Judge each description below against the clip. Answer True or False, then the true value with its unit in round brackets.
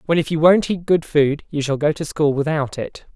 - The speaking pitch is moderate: True (155 Hz)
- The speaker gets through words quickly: True (265 wpm)